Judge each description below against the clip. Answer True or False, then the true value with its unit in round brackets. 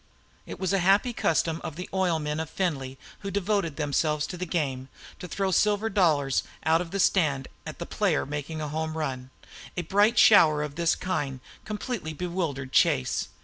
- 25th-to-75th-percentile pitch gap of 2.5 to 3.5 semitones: False (4.2 semitones)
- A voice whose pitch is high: False (160 Hz)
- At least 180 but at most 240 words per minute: True (185 wpm)